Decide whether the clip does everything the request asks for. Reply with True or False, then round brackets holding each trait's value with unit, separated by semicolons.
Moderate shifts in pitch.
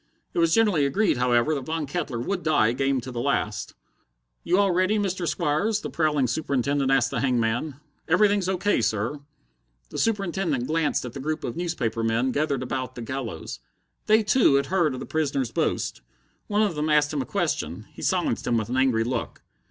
False (5.8 semitones)